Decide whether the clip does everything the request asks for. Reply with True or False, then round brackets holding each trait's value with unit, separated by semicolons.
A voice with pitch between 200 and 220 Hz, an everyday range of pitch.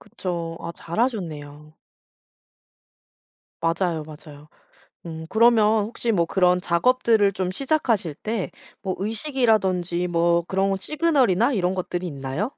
False (185 Hz; 4.7 semitones)